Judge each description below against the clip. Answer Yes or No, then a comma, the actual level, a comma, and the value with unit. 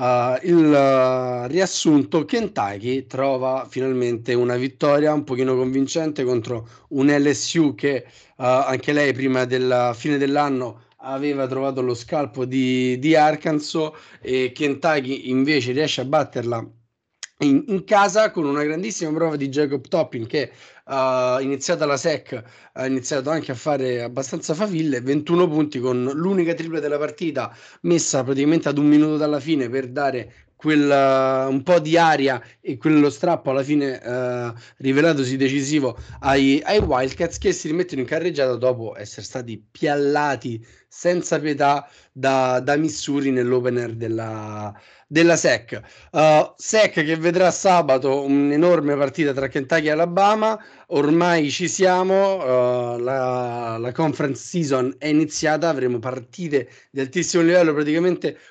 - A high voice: No, medium, 140 Hz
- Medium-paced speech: Yes, average, 140 wpm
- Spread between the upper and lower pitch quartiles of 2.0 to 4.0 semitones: Yes, average, 3.7 semitones